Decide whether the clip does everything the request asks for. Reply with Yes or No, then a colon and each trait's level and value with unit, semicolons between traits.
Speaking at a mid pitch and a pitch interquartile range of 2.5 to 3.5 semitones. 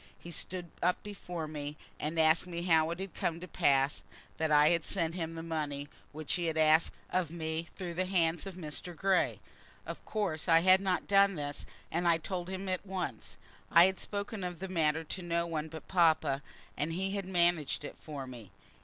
Yes: medium, 170 Hz; average, 2.8 semitones